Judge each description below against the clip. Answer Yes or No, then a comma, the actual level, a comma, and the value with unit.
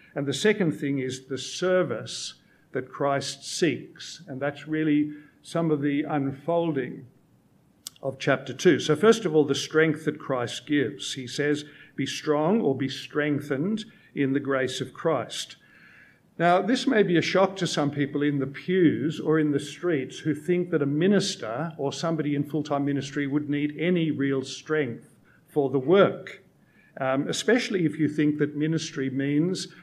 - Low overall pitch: No, medium, 150 Hz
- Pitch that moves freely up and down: No, average, 3.2 semitones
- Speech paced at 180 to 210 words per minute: No, average, 170 wpm